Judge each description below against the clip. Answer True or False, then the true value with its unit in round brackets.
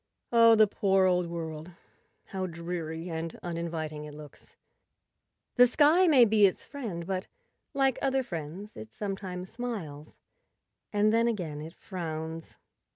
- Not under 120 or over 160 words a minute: True (135 wpm)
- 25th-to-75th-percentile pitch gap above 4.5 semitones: True (5.3 semitones)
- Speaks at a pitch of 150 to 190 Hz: True (185 Hz)